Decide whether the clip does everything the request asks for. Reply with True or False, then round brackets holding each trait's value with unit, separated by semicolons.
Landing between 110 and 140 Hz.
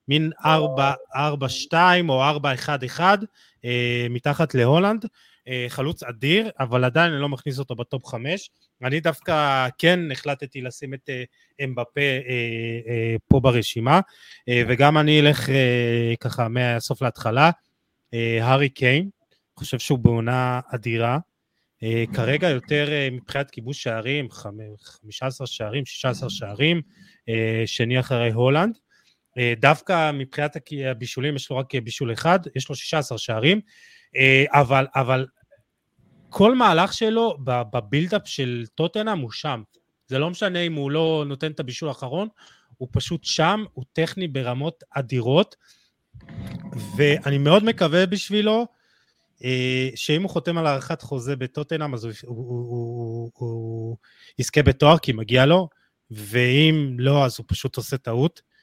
True (135 Hz)